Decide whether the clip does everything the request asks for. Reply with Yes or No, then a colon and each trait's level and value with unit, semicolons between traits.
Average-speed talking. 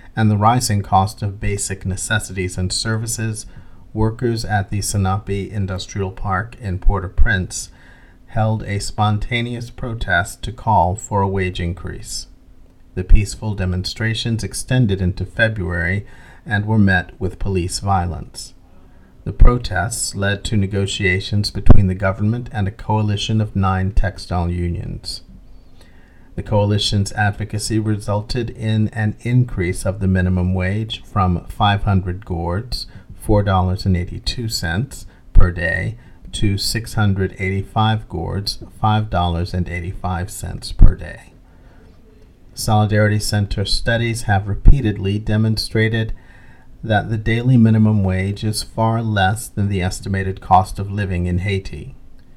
No: slow, 115 wpm